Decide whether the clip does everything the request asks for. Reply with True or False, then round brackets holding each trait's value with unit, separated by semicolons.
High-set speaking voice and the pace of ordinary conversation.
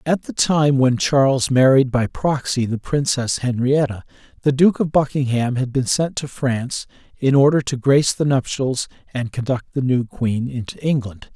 False (130 Hz; 175 wpm)